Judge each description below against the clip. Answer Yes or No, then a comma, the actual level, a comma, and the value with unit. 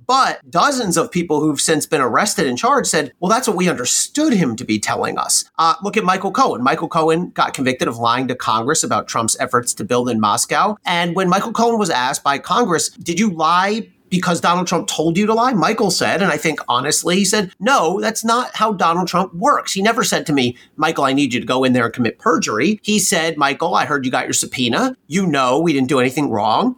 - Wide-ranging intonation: Yes, wide, 7.0 semitones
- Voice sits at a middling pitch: Yes, medium, 175 Hz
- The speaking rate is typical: No, fast, 240 wpm